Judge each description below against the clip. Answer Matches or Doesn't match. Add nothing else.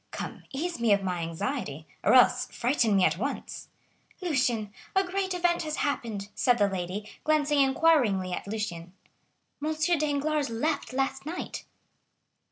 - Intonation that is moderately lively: Doesn't match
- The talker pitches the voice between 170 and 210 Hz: Doesn't match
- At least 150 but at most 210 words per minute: Doesn't match